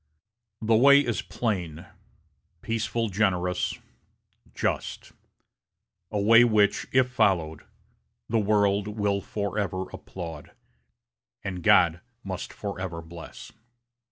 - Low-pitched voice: Yes, low, 100 Hz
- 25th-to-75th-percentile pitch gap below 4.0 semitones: Yes, average, 3.4 semitones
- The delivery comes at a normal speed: No, slow, 95 wpm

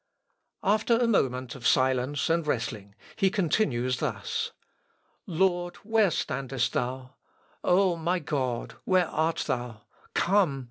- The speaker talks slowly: Yes, slow, 120 wpm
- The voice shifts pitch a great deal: Yes, wide, 6.6 semitones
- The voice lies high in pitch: No, medium, 150 Hz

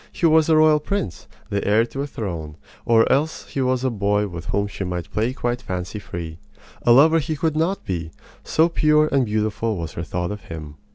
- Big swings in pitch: Yes, wide, 8.8 semitones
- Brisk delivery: Yes, fast, 215 wpm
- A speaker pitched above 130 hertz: No, low, 115 Hz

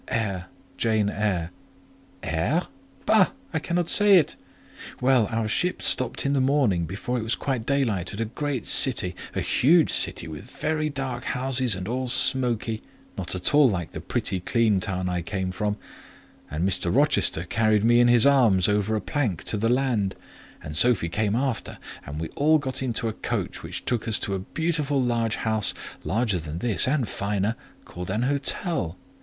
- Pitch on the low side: Yes, low, 115 Hz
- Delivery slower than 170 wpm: No, average, 175 wpm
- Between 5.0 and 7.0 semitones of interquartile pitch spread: Yes, wide, 5.4 semitones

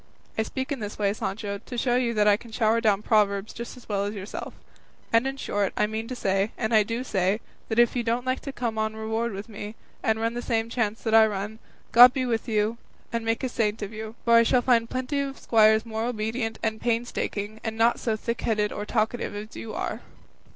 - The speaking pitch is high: Yes, high, 225 Hz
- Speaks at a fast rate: Yes, fast, 235 wpm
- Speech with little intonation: Yes, narrow, 1.8 semitones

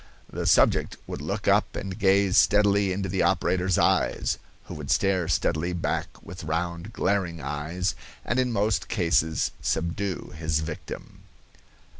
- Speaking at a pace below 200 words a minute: Yes, average, 140 wpm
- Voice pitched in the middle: No, very low, 90 Hz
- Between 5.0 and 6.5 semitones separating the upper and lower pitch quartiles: No, average, 3.2 semitones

